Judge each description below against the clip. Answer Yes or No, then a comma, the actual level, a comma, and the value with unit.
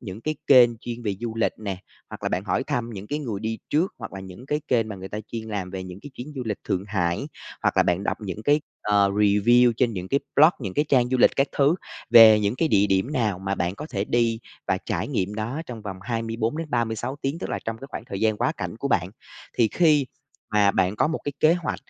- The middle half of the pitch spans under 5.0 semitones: Yes, average, 4.5 semitones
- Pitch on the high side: No, low, 110 Hz